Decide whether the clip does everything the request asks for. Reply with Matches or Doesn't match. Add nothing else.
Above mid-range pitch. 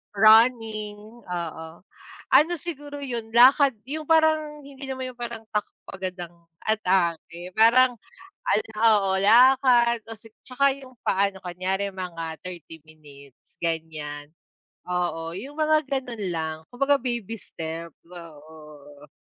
Matches